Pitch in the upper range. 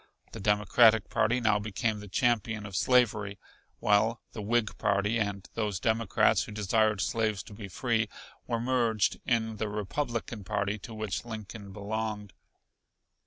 No: low, 110 Hz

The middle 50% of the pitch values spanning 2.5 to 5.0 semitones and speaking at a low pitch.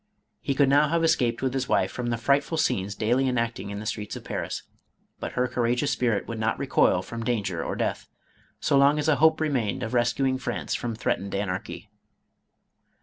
Yes: average, 3.8 semitones; low, 125 Hz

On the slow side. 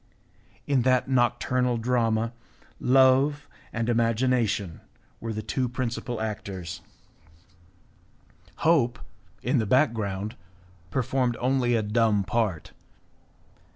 Yes: slow, 90 wpm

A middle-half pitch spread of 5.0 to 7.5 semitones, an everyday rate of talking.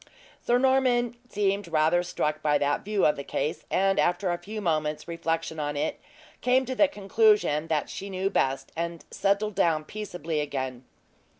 Yes: wide, 5.4 semitones; average, 170 wpm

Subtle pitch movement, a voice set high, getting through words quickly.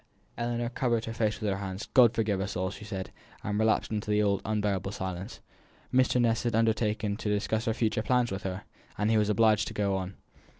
No: narrow, 2.3 semitones; low, 105 Hz; fast, 215 wpm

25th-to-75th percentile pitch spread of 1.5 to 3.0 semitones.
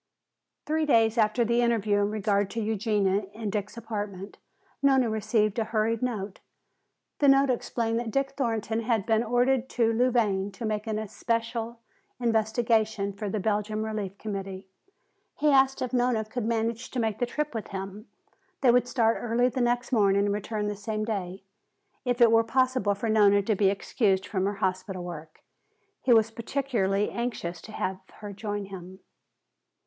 Yes: average, 2.7 semitones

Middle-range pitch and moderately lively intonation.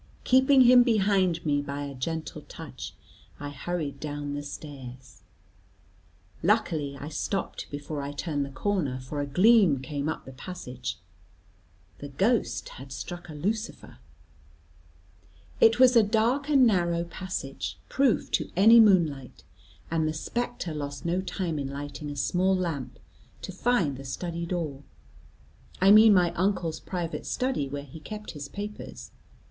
No: medium, 165 Hz; wide, 6.0 semitones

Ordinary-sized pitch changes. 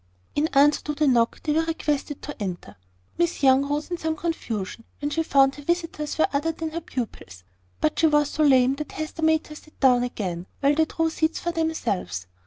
Yes: average, 3.8 semitones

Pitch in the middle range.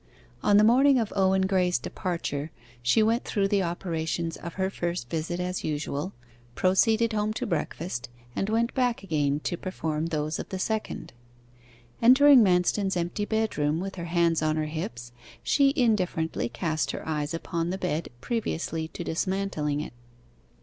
Yes: medium, 180 Hz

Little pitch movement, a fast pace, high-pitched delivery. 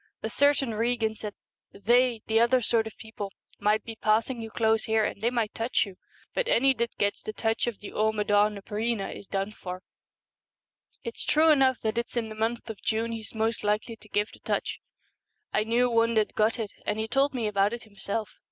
Yes: narrow, 1.9 semitones; fast, 215 wpm; high, 220 Hz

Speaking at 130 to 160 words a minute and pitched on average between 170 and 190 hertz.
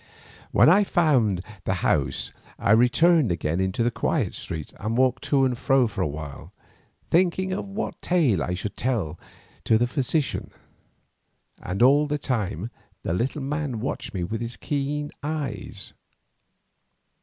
No: average, 155 wpm; low, 125 Hz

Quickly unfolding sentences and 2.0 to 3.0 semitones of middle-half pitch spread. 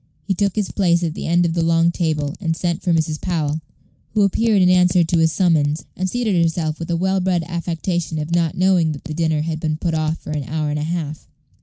Yes: fast, 245 wpm; narrow, 2.4 semitones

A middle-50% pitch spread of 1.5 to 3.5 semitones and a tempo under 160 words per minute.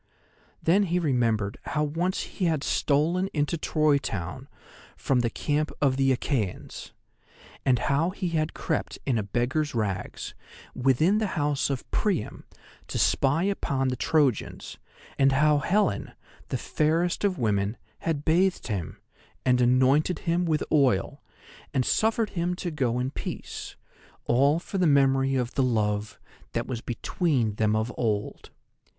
No: average, 5.0 semitones; average, 145 wpm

